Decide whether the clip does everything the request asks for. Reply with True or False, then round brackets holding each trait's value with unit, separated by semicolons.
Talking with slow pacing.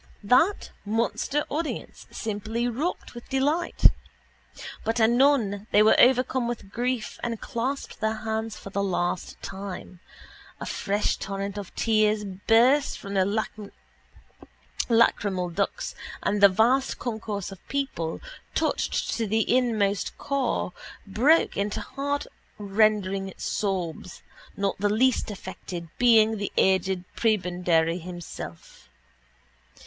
True (110 wpm)